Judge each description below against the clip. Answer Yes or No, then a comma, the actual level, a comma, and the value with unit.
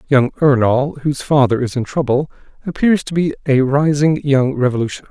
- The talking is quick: No, average, 165 wpm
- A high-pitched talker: No, medium, 140 Hz